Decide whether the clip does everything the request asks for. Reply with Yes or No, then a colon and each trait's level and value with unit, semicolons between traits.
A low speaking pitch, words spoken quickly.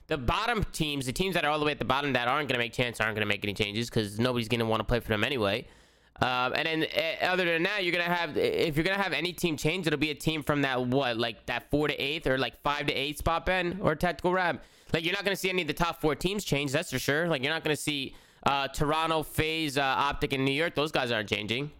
No: medium, 150 Hz; fast, 285 wpm